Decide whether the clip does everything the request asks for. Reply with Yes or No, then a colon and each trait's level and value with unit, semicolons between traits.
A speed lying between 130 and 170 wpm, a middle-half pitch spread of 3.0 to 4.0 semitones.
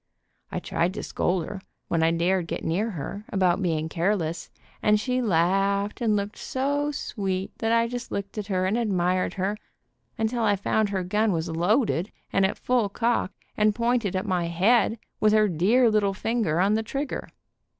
No: average, 185 wpm; average, 3.5 semitones